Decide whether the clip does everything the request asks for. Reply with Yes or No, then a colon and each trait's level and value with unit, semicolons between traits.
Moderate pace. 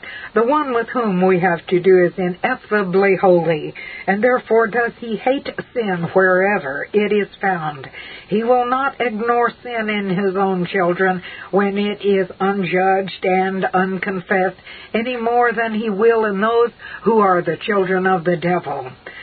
Yes: average, 155 wpm